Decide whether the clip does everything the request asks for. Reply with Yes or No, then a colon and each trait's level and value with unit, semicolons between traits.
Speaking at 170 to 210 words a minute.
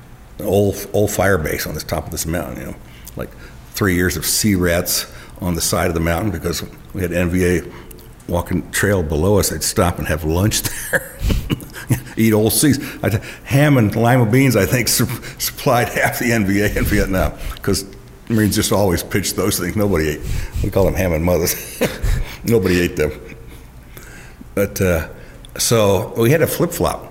Yes: average, 180 wpm